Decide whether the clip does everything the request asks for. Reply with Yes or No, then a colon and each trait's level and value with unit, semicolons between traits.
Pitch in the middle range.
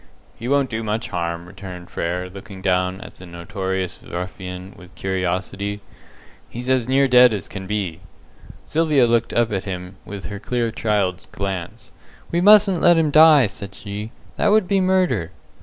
No: low, 100 Hz